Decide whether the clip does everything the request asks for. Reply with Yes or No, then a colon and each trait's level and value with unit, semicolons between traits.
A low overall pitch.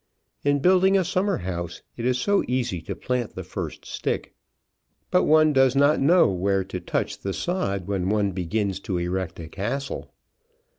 Yes: low, 115 Hz